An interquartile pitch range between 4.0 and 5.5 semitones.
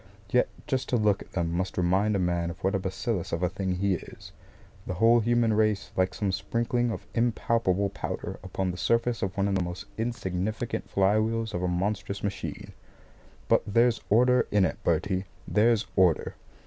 No: average, 3.6 semitones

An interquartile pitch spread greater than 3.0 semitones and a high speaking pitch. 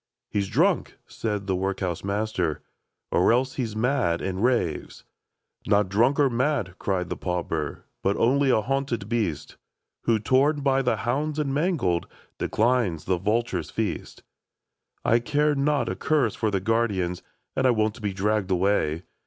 No: wide, 5.5 semitones; low, 110 Hz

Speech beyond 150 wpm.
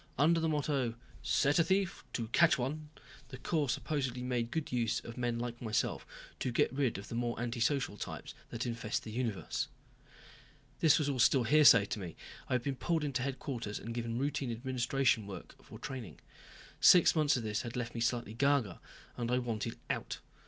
Yes: average, 190 wpm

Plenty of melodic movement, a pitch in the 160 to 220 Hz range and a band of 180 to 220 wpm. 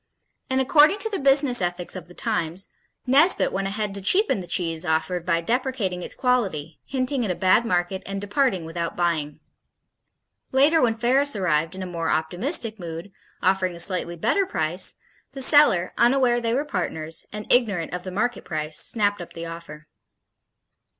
No: wide, 6.6 semitones; high, 190 Hz; average, 170 wpm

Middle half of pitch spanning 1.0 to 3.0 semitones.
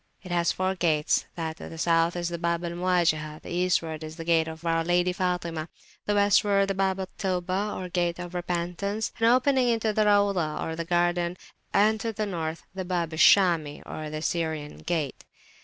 Yes: narrow, 2.6 semitones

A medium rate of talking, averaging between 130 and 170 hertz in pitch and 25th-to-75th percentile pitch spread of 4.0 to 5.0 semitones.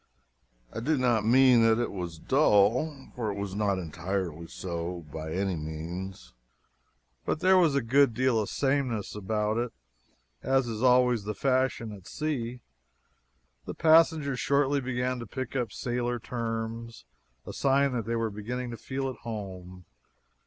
No: average, 155 wpm; low, 115 Hz; average, 4.6 semitones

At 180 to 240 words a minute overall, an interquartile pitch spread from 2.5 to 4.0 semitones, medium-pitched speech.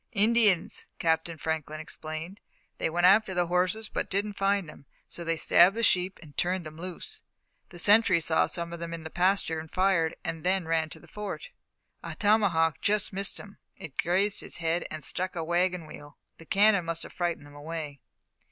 Yes: average, 190 wpm; average, 3.3 semitones; medium, 175 Hz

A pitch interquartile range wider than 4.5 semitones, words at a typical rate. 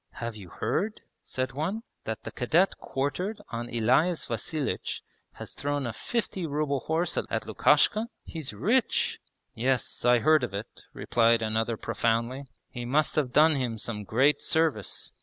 Yes: average, 5.3 semitones; average, 155 wpm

